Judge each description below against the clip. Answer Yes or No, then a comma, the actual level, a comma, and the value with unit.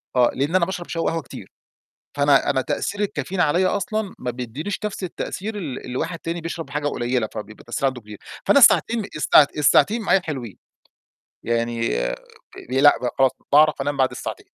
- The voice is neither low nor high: Yes, medium, 145 Hz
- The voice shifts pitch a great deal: Yes, wide, 6.2 semitones